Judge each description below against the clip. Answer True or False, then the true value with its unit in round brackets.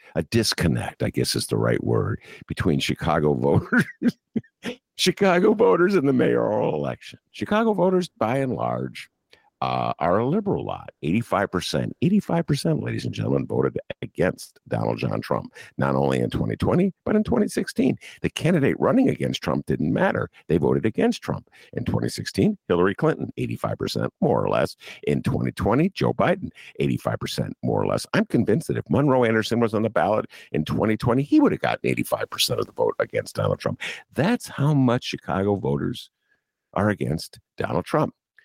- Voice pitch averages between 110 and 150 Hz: True (135 Hz)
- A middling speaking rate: True (160 wpm)